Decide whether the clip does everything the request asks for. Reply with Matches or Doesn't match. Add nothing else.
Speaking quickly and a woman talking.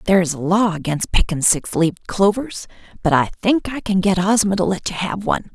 Matches